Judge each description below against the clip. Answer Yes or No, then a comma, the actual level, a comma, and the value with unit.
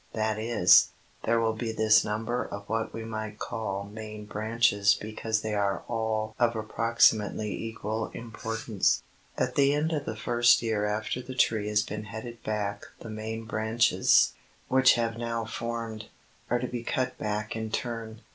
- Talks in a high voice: No, low, 110 Hz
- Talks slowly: No, average, 165 wpm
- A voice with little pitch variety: Yes, narrow, 1.4 semitones